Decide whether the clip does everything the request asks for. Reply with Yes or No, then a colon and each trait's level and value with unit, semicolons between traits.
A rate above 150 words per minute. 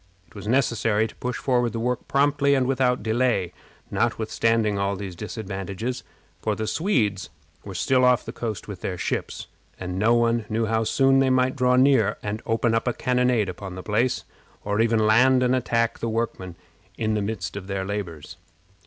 Yes: average, 185 wpm